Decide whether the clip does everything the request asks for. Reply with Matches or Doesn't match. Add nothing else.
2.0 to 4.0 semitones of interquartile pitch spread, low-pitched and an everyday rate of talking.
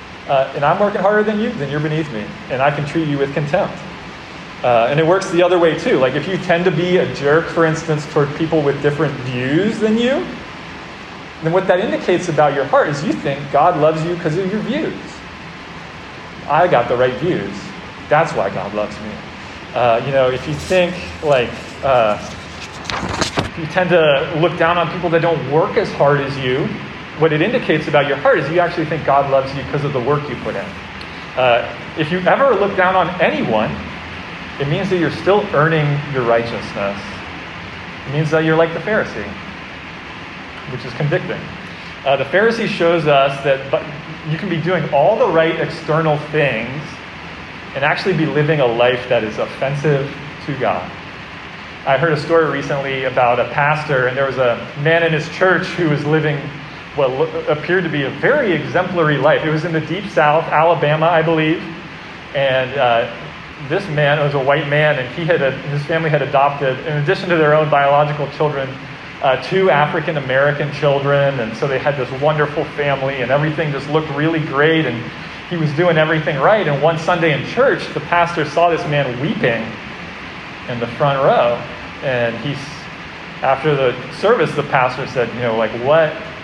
Doesn't match